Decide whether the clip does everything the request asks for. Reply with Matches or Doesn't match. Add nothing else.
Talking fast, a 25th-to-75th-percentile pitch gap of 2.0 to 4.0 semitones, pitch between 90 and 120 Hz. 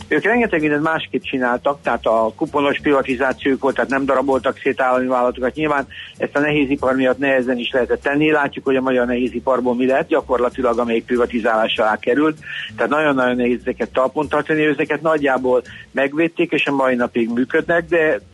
Doesn't match